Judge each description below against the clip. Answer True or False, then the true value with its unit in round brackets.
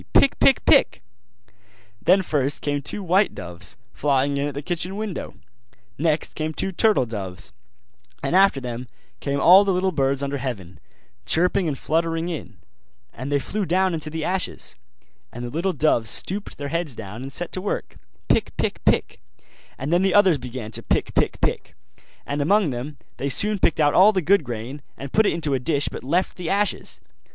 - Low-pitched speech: False (155 Hz)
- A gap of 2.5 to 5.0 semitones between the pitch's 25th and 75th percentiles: False (5.4 semitones)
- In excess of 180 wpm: True (190 wpm)